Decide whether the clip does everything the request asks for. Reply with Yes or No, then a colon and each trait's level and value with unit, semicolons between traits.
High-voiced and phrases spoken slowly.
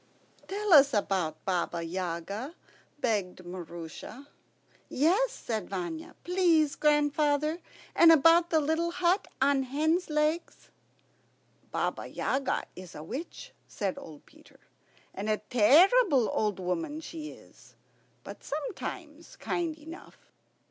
Yes: very high, 285 Hz; slow, 110 wpm